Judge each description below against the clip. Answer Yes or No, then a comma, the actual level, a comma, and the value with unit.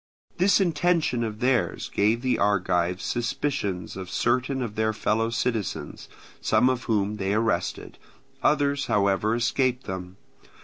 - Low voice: Yes, low, 115 Hz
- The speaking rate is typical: No, slow, 130 wpm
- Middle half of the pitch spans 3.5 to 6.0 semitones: Yes, average, 4.2 semitones